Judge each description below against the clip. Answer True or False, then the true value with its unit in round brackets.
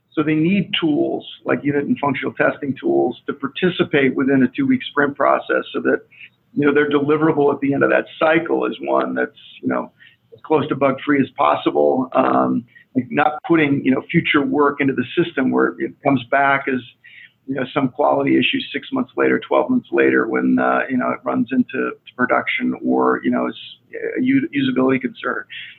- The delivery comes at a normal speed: True (190 wpm)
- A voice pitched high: False (140 Hz)